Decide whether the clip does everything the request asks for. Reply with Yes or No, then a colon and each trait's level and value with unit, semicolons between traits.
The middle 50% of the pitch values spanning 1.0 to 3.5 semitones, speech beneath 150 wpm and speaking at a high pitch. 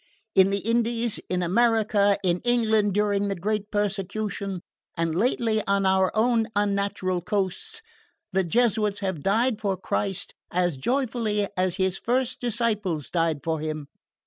Yes: average, 3.2 semitones; average, 140 wpm; high, 200 Hz